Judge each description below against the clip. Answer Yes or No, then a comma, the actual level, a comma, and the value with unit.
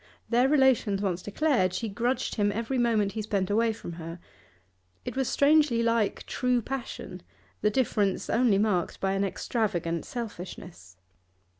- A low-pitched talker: No, high, 215 Hz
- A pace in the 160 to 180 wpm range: No, average, 145 wpm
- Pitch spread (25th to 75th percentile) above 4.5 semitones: No, average, 3.9 semitones